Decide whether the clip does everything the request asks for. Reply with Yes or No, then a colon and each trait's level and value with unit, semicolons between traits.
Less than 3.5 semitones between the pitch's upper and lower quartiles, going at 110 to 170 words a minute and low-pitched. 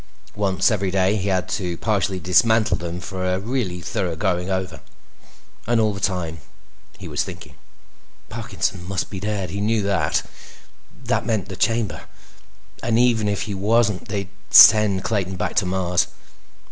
Yes: narrow, 2.6 semitones; average, 160 wpm; very low, 95 Hz